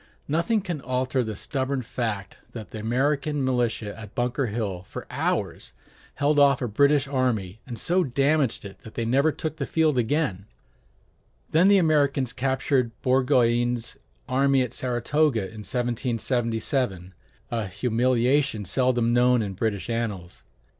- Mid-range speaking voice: No, low, 125 Hz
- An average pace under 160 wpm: Yes, average, 140 wpm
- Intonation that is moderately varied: Yes, average, 3.8 semitones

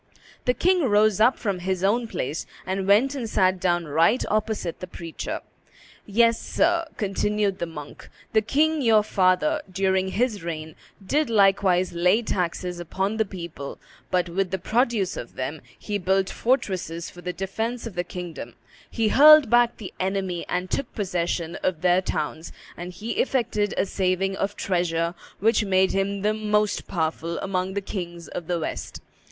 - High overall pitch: Yes, high, 195 Hz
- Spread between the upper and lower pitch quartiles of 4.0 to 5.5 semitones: No, average, 3.6 semitones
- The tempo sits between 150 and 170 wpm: Yes, average, 165 wpm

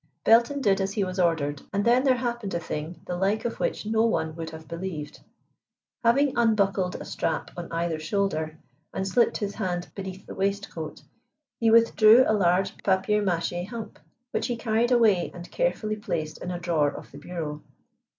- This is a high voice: Yes, high, 195 Hz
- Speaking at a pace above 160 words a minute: Yes, average, 180 wpm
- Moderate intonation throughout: Yes, average, 4.6 semitones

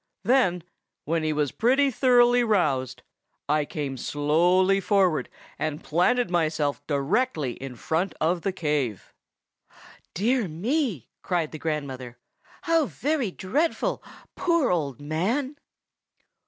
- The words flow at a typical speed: No, slow, 115 wpm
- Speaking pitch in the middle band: Yes, medium, 175 Hz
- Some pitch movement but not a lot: No, wide, 8.3 semitones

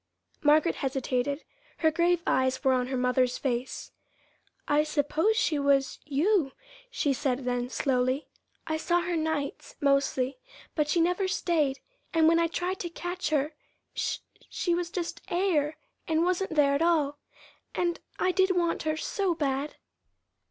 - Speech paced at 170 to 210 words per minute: No, average, 150 wpm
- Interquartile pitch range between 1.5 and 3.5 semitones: No, average, 4.0 semitones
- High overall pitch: Yes, very high, 305 Hz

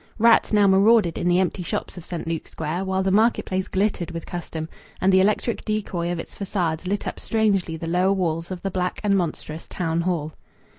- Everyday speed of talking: No, fast, 210 wpm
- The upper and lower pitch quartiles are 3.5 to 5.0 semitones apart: No, average, 2.8 semitones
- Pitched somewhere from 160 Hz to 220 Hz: Yes, medium, 185 Hz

